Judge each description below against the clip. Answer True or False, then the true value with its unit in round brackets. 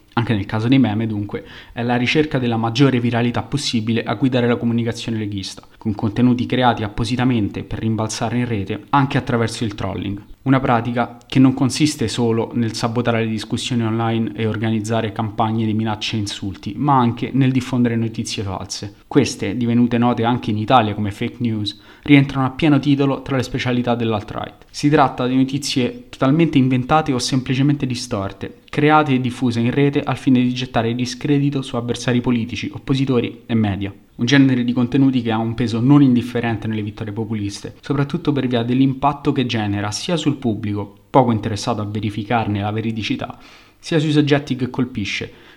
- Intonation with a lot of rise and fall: False (3.0 semitones)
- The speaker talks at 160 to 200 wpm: True (170 wpm)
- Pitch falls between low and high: False (120 Hz)